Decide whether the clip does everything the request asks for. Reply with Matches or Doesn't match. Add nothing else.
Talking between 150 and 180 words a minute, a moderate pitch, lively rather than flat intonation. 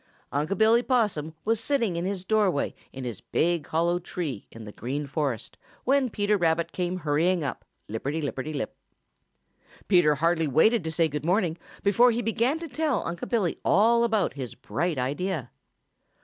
Matches